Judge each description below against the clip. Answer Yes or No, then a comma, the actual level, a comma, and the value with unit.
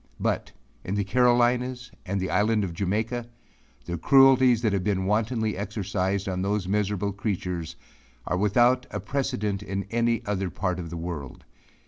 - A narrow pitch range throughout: No, average, 4.0 semitones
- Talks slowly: No, average, 155 wpm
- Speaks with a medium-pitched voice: No, low, 105 Hz